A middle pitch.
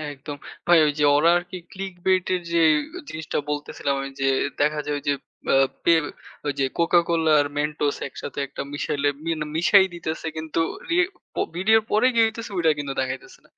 Yes: medium, 160 Hz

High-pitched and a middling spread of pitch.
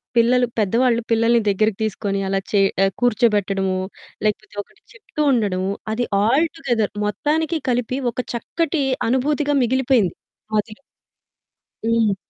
Yes: high, 230 Hz; average, 3.7 semitones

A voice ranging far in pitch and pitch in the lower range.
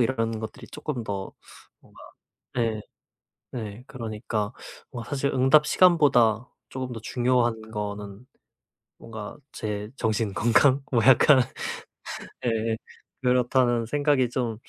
No: average, 2.8 semitones; low, 120 Hz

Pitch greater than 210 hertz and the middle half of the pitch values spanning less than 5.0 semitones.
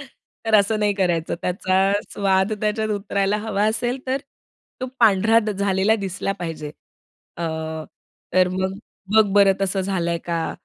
No: high, 195 Hz; narrow, 2.4 semitones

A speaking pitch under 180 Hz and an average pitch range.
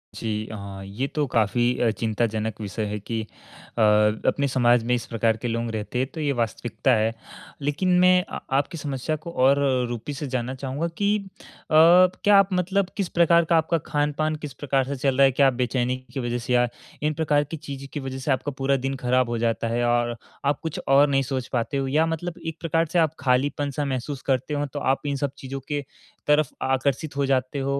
Yes: low, 135 Hz; average, 3.7 semitones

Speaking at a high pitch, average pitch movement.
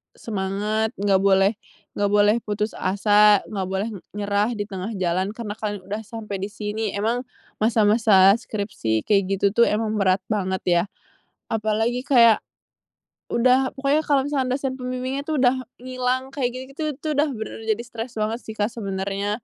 Yes: high, 215 Hz; average, 3.6 semitones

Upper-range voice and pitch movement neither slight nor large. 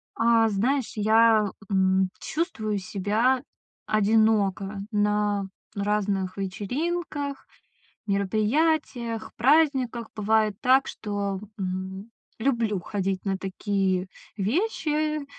Yes: high, 215 Hz; average, 3.9 semitones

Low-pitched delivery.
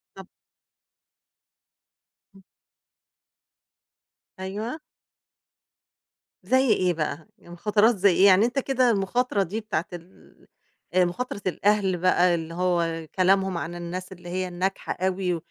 No: medium, 185 Hz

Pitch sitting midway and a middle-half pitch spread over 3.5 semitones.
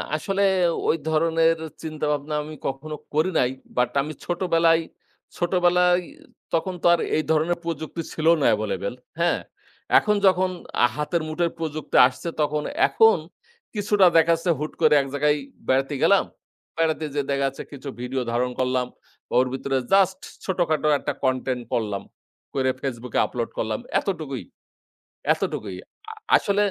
Yes: medium, 155 Hz; average, 4.3 semitones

